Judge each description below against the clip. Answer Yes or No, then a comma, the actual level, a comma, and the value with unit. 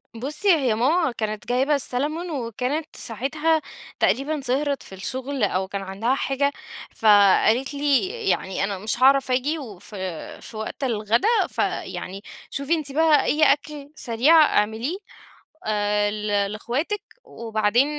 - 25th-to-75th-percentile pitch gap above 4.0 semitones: Yes, average, 5.3 semitones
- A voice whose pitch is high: Yes, very high, 255 Hz